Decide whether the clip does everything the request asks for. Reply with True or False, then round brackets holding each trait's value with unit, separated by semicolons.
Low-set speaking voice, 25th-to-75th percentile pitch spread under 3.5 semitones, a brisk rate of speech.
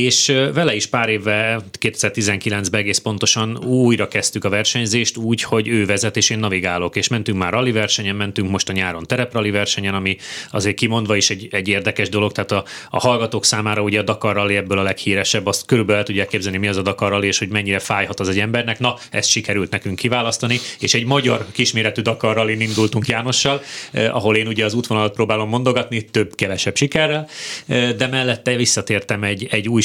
True (110 Hz; 2.7 semitones; 190 wpm)